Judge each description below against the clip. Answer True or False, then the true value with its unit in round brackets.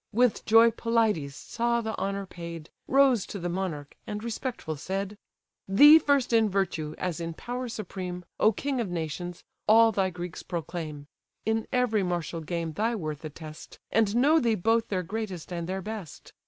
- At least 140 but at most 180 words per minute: True (170 wpm)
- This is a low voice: False (195 Hz)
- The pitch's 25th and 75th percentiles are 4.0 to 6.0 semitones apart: True (5.0 semitones)